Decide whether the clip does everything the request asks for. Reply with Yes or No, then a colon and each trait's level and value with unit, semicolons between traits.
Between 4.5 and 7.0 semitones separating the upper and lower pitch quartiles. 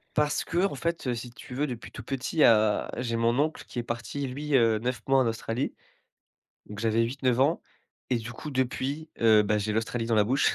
No: average, 3.5 semitones